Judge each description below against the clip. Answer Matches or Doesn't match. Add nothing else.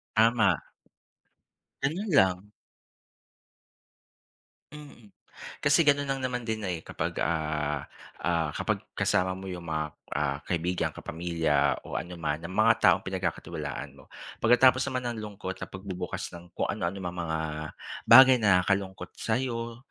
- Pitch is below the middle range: Matches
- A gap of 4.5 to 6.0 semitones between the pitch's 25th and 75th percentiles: Matches